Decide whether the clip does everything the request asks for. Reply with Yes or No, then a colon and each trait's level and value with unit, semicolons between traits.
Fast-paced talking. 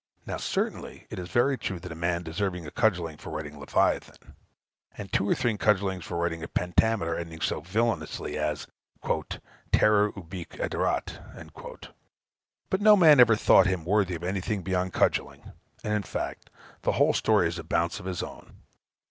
No: average, 170 wpm